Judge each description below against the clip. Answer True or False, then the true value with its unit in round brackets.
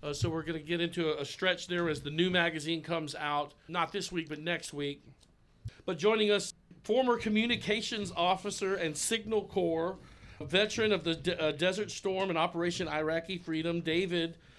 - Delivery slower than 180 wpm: False (185 wpm)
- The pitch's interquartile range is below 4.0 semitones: True (3.3 semitones)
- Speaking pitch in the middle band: True (170 Hz)